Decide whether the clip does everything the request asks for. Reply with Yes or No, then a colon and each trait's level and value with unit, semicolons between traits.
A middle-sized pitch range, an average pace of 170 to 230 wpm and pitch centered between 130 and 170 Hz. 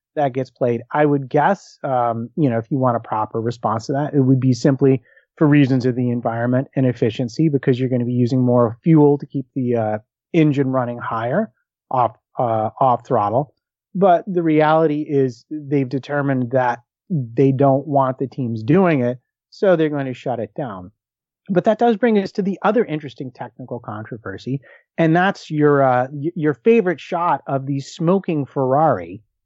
Yes: average, 3.8 semitones; average, 185 wpm; low, 135 Hz